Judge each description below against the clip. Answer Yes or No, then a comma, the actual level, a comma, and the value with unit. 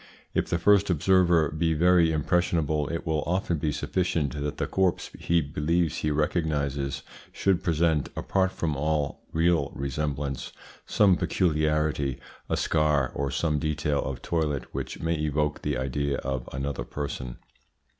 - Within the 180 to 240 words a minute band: No, average, 145 wpm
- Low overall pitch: Yes, very low, 75 Hz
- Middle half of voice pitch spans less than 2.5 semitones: No, average, 2.8 semitones